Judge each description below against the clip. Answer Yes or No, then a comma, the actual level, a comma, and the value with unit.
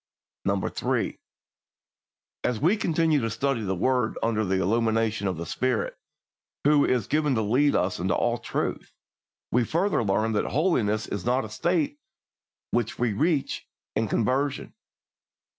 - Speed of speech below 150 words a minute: Yes, average, 140 wpm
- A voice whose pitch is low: Yes, low, 120 Hz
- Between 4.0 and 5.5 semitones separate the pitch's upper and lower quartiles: Yes, average, 5.2 semitones